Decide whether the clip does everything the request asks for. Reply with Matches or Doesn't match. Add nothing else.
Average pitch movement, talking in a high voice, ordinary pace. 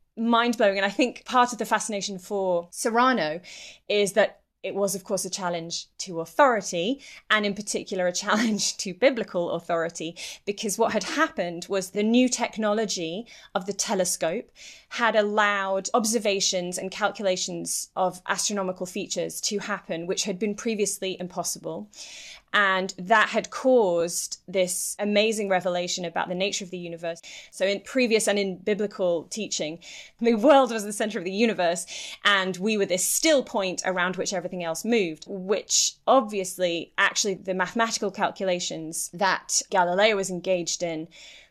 Matches